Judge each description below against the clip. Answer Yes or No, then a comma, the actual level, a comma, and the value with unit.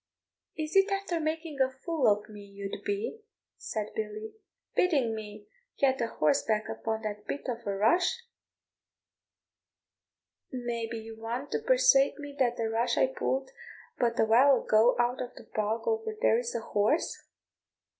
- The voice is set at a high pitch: Yes, high, 240 Hz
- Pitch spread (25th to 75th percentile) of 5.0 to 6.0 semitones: Yes, wide, 5.5 semitones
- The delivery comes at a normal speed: Yes, average, 160 wpm